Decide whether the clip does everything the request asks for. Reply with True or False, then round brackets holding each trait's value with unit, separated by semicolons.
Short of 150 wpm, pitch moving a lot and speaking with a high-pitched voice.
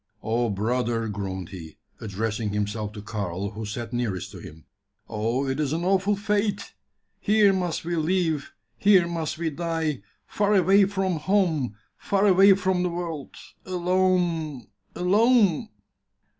False (140 wpm; 9.0 semitones; 160 Hz)